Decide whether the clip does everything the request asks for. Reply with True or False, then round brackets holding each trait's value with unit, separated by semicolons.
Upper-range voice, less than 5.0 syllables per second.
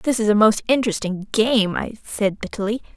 False (215 Hz; 5.4 syllables/s)